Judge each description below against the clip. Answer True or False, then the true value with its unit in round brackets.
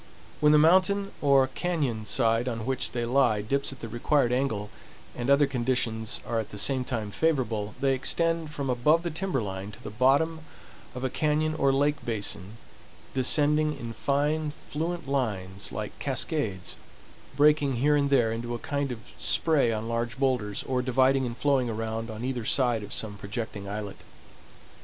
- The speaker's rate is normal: True (170 wpm)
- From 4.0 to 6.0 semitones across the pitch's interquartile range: True (4.3 semitones)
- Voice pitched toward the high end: False (130 Hz)